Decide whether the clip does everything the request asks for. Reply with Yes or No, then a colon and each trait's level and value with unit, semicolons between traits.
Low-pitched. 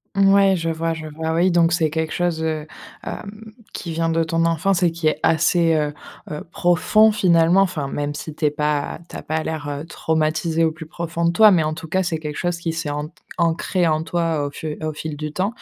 No: medium, 165 Hz